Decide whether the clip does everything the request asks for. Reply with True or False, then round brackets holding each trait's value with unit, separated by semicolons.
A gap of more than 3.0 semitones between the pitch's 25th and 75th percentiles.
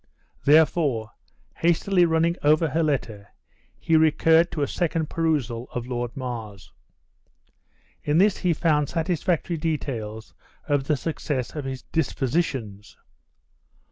True (5.0 semitones)